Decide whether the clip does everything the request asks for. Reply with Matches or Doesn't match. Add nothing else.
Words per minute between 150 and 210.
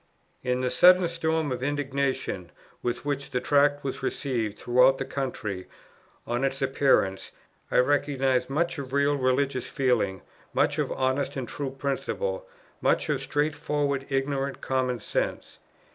Doesn't match